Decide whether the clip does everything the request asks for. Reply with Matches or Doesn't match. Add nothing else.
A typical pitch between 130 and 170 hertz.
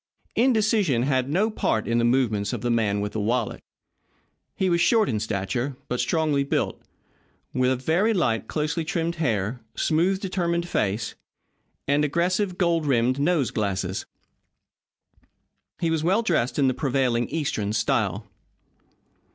Matches